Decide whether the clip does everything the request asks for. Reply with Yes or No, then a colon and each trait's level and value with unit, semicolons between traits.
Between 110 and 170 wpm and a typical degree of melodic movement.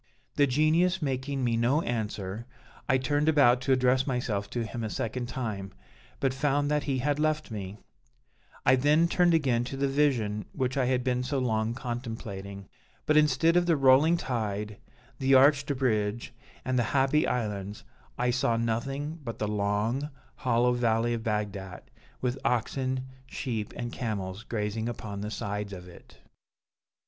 Yes: average, 160 wpm; average, 4.0 semitones